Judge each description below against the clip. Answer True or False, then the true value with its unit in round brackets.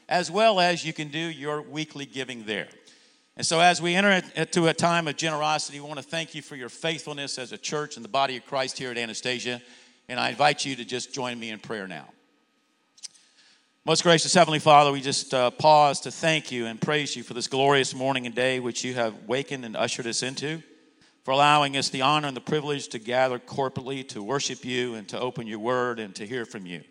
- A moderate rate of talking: False (225 wpm)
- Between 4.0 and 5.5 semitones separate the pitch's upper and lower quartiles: False (3.5 semitones)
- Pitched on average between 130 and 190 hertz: True (140 Hz)